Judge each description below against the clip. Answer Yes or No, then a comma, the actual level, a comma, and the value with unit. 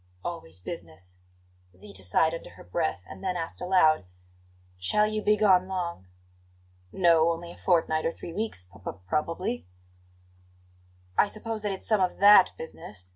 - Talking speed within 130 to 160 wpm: Yes, average, 150 wpm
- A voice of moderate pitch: Yes, medium, 165 Hz